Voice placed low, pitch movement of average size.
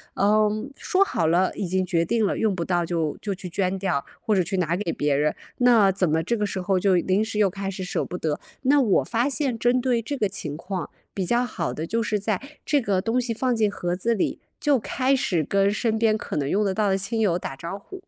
No: high, 200 Hz; average, 4.1 semitones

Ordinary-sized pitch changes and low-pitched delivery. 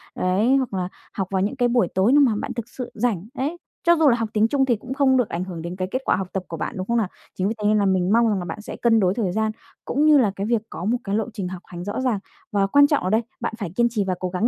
No: average, 4.6 semitones; high, 215 Hz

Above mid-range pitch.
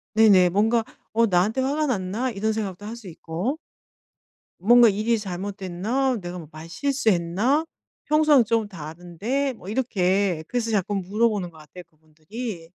Yes: high, 205 Hz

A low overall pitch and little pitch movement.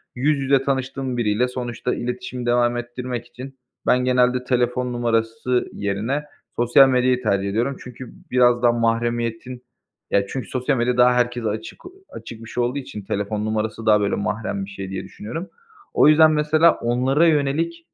Yes: low, 120 Hz; narrow, 2.2 semitones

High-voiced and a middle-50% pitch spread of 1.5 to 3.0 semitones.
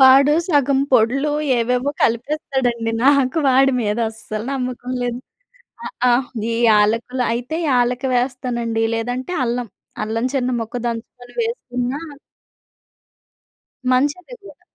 Yes: very high, 250 Hz; narrow, 2.4 semitones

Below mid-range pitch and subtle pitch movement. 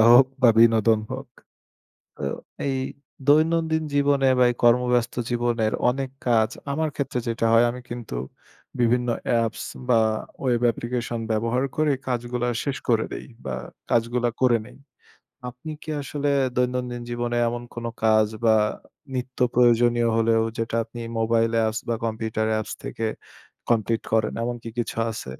Yes: low, 120 Hz; narrow, 1.7 semitones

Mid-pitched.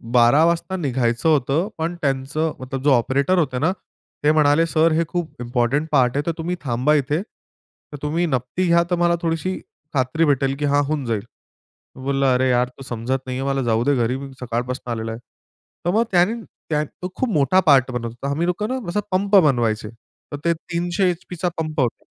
Yes: medium, 145 Hz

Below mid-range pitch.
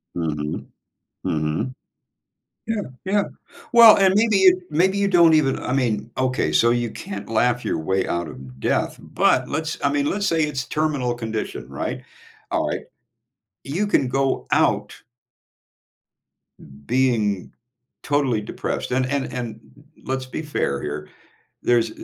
Yes: low, 130 Hz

